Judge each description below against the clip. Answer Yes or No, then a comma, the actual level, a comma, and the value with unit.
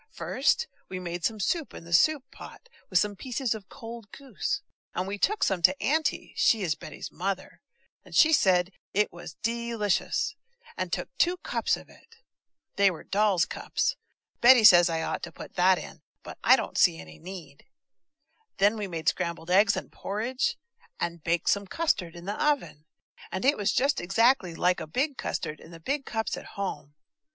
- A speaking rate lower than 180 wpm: No, average, 185 wpm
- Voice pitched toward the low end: No, high, 200 Hz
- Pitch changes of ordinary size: No, wide, 5.8 semitones